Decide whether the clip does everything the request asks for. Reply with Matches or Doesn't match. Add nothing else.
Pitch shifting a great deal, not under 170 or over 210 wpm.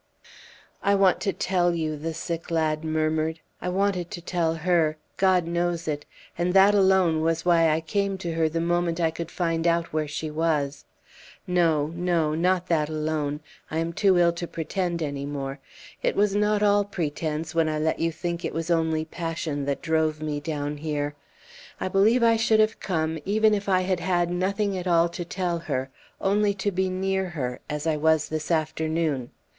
Doesn't match